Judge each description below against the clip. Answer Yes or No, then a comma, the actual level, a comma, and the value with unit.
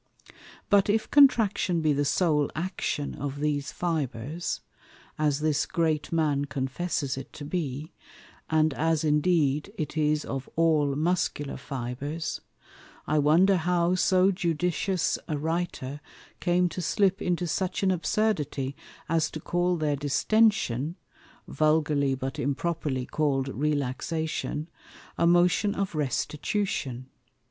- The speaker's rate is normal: No, slow, 120 wpm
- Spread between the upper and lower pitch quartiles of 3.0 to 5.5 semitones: Yes, average, 3.6 semitones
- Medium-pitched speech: Yes, medium, 155 Hz